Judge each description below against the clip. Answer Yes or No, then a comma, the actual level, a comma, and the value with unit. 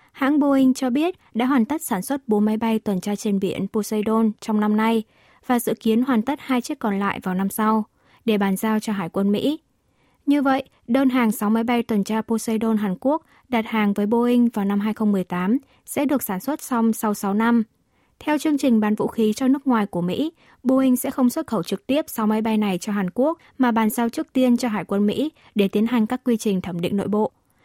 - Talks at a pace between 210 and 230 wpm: No, average, 240 wpm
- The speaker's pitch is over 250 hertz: No, high, 225 Hz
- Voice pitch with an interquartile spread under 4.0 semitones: Yes, average, 3.6 semitones